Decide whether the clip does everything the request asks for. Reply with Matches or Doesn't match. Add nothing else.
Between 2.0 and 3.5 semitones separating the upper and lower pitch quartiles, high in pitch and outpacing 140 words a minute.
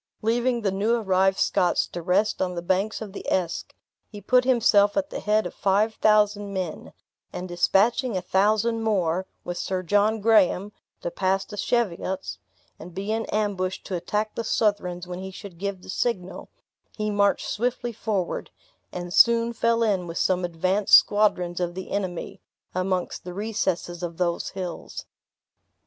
Matches